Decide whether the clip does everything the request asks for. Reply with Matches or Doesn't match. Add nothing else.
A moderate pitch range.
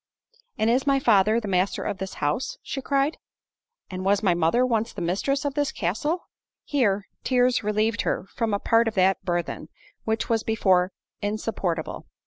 Matches